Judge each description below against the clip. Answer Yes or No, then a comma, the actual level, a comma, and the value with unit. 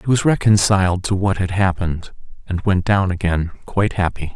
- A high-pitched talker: No, very low, 95 Hz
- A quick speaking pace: No, average, 180 wpm